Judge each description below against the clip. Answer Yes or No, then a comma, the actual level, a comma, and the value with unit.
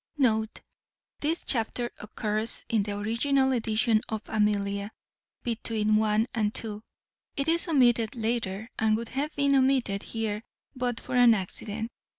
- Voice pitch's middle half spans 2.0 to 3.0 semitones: Yes, average, 2.7 semitones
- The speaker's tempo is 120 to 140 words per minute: Yes, slow, 135 wpm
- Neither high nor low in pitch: No, high, 225 Hz